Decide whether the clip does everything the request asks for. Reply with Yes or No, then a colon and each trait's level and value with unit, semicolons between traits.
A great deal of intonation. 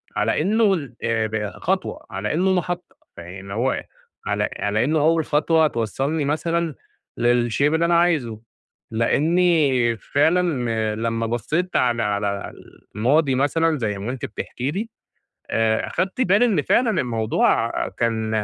Yes: wide, 6.7 semitones